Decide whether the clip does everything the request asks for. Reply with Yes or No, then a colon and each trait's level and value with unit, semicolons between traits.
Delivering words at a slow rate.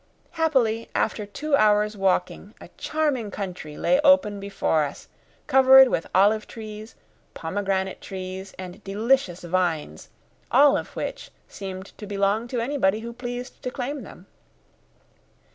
Yes: slow, 130 wpm